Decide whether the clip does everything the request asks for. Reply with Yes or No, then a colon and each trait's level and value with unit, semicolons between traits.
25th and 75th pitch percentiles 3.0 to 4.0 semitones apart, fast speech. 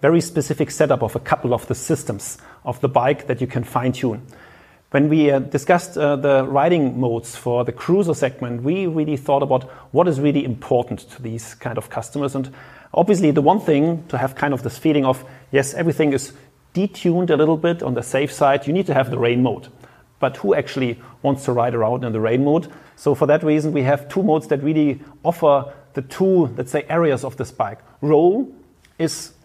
Yes: average, 3.4 semitones; fast, 210 wpm